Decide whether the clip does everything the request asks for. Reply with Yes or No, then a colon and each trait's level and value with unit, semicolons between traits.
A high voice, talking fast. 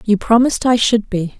Yes: high, 225 Hz; fast, 215 wpm